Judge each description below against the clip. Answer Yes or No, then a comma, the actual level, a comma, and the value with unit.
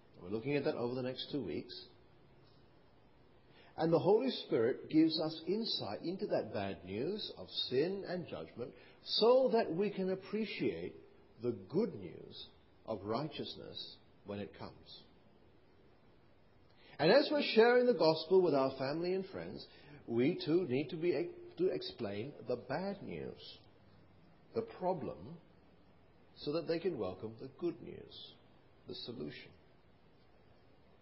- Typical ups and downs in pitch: No, wide, 7.9 semitones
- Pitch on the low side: No, medium, 180 Hz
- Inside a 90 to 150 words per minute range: Yes, slow, 135 wpm